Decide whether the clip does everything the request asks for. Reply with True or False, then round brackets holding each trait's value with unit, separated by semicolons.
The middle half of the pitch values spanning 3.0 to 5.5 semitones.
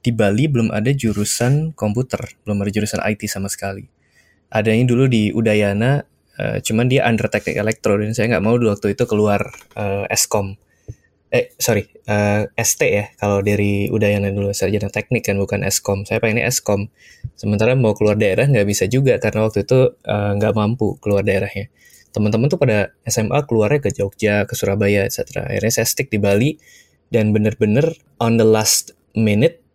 False (2.6 semitones)